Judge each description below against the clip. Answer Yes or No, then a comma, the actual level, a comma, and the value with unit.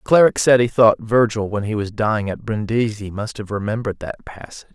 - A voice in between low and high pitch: No, low, 110 Hz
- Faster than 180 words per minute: Yes, average, 200 wpm